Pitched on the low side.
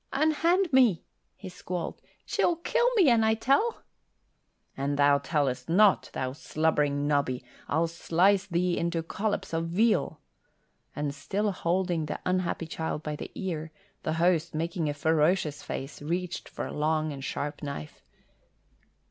No: medium, 165 Hz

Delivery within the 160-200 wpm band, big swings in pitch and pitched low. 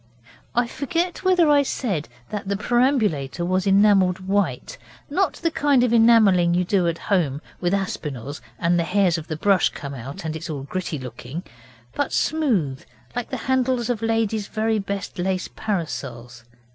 No: average, 165 wpm; wide, 6.1 semitones; high, 195 Hz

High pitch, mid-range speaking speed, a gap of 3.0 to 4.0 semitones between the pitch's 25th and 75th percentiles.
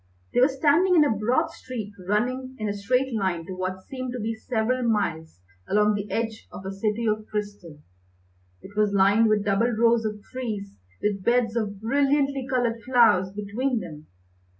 Yes: high, 220 Hz; average, 175 wpm; average, 3.7 semitones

